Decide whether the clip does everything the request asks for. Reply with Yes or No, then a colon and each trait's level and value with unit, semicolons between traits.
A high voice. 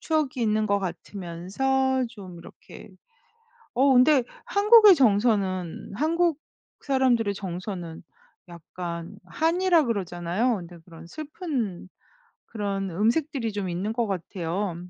Yes: high, 210 Hz